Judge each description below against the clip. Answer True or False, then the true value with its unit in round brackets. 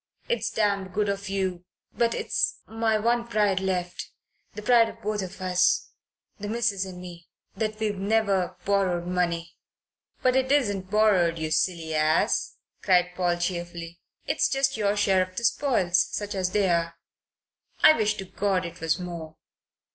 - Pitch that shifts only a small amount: False (3.3 semitones)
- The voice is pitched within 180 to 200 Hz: True (190 Hz)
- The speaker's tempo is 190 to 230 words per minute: False (165 wpm)